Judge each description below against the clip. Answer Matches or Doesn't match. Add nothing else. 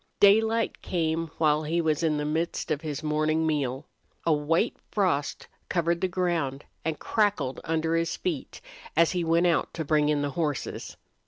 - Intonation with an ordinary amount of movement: Doesn't match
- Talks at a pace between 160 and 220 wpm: Matches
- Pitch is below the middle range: Doesn't match